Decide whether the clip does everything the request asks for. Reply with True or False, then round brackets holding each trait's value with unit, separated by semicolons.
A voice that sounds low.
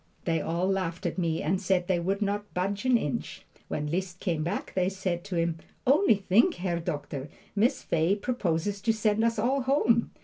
False (190 Hz)